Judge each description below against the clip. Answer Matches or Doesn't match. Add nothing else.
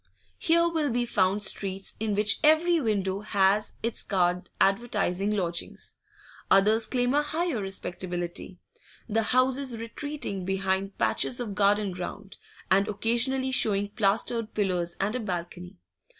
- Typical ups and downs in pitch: Matches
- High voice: Matches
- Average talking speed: Doesn't match